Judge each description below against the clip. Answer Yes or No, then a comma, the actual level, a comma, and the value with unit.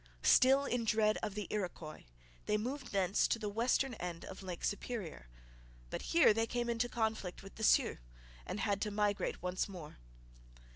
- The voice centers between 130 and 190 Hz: No, high, 210 Hz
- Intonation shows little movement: No, average, 3.3 semitones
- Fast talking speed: No, average, 175 wpm